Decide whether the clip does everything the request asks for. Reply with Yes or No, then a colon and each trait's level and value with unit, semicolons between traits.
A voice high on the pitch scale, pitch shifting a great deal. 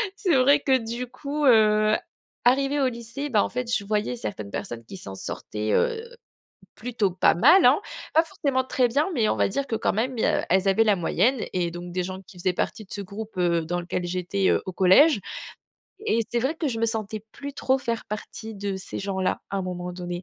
Yes: high, 215 Hz; wide, 5.8 semitones